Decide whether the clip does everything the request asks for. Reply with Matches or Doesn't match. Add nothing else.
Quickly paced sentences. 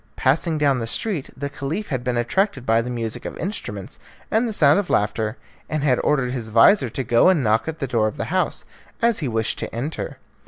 Matches